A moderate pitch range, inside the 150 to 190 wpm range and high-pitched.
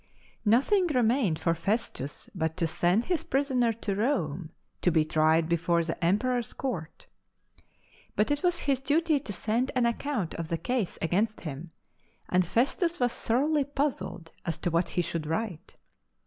No: wide, 7.8 semitones; average, 160 wpm; high, 210 Hz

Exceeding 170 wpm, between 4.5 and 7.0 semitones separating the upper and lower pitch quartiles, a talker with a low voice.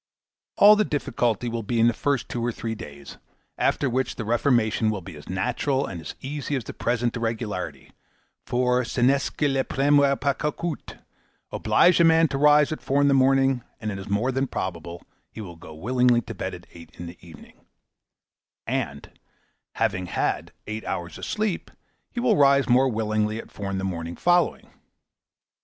Yes: average, 185 wpm; average, 5.1 semitones; low, 120 Hz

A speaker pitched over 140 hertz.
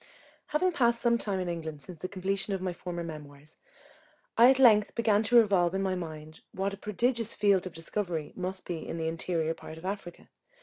Yes: medium, 185 Hz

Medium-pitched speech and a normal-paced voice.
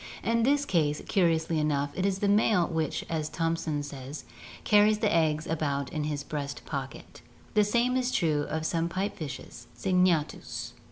Yes: medium, 165 Hz; average, 170 wpm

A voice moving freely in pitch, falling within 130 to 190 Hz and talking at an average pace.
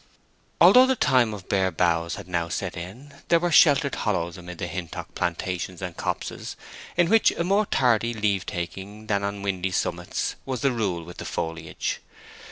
No: wide, 6.4 semitones; low, 100 Hz; average, 175 wpm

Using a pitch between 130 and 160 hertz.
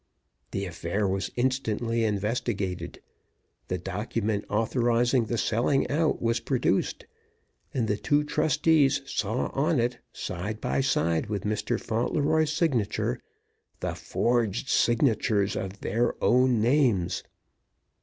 No: low, 115 Hz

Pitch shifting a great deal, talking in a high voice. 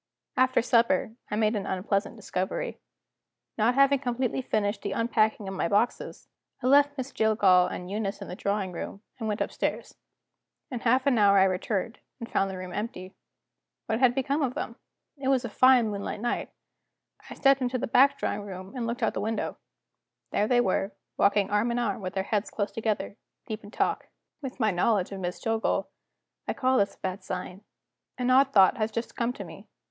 No: average, 3.8 semitones; high, 220 Hz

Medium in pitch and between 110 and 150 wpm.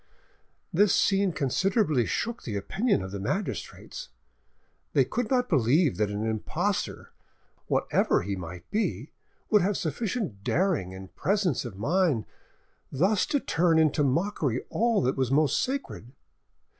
Yes: medium, 155 Hz; slow, 135 wpm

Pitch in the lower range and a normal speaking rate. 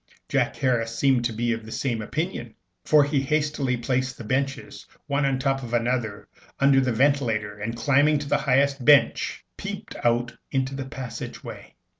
Yes: low, 130 Hz; average, 185 wpm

